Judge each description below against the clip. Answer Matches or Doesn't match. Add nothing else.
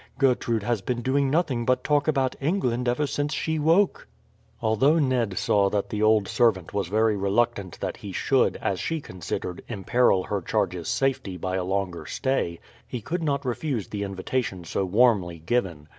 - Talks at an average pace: Matches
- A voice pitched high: Doesn't match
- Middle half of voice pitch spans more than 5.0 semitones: Matches